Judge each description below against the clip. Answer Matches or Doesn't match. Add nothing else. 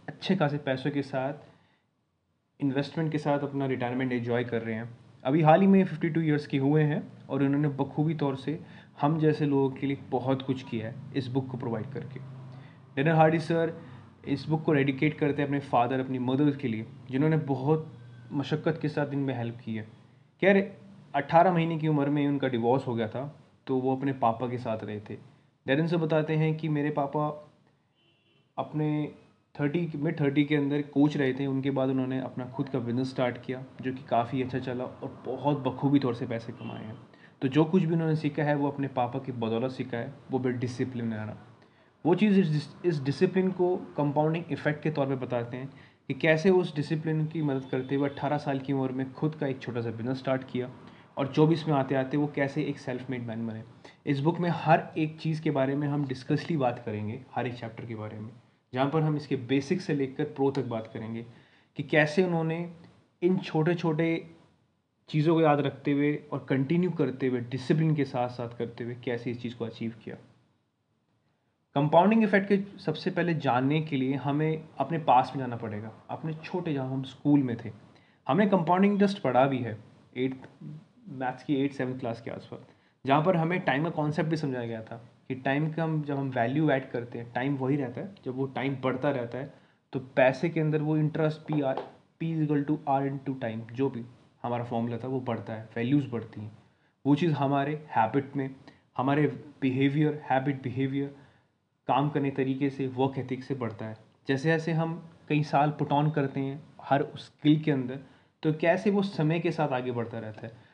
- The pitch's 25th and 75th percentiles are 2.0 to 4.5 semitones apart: Matches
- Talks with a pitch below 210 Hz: Matches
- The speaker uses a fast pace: Matches